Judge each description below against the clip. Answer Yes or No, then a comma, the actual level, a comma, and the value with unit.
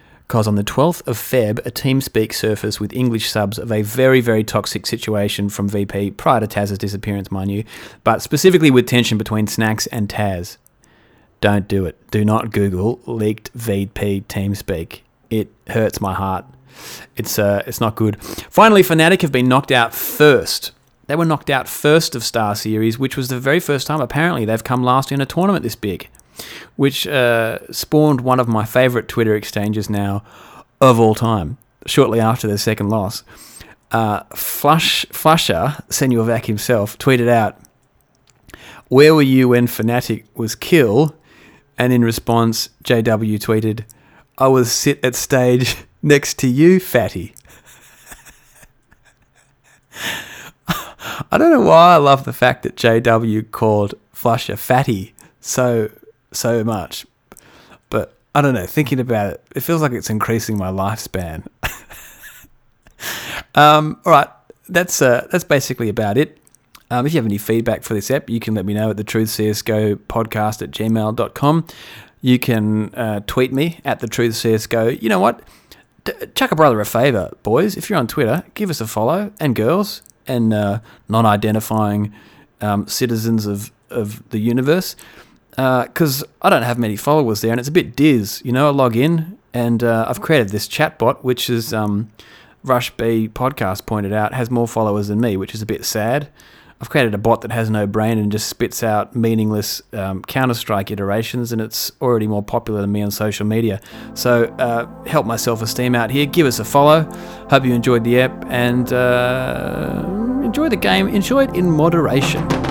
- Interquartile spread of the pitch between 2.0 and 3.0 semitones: No, average, 3.9 semitones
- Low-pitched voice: Yes, low, 115 Hz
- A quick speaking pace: No, average, 175 wpm